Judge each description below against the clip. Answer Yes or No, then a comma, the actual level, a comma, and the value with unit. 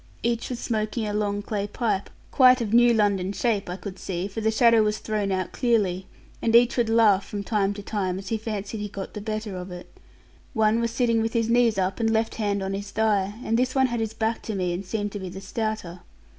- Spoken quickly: Yes, fast, 240 wpm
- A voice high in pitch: Yes, high, 215 Hz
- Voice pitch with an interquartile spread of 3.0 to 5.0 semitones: No, narrow, 2.5 semitones